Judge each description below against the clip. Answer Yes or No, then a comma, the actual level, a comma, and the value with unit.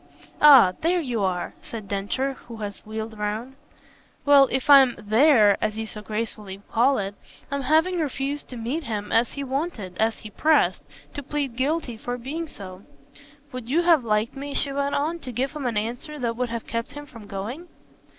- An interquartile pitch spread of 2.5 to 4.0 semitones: No, average, 4.7 semitones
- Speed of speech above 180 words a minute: Yes, average, 190 wpm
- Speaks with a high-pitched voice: Yes, high, 245 Hz